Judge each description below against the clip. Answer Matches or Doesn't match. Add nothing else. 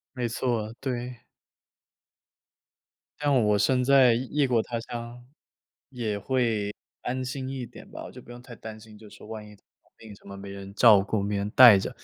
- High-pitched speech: Doesn't match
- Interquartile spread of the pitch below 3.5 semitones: Matches